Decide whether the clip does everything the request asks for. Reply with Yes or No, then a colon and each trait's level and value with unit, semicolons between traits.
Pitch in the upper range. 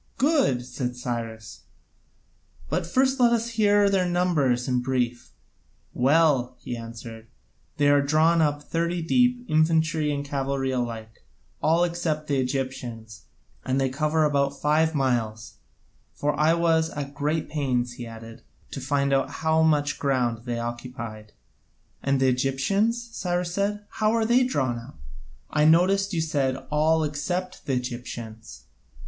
No: medium, 145 Hz